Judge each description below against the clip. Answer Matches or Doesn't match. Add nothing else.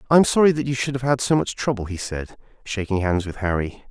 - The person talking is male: Matches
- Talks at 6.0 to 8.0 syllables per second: Matches